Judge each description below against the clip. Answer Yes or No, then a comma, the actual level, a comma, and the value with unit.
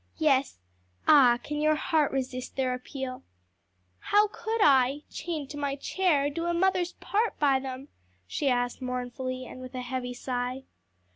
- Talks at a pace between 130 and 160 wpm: Yes, average, 155 wpm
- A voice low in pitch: No, very high, 270 Hz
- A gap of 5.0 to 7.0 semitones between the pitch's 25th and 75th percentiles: No, average, 3.3 semitones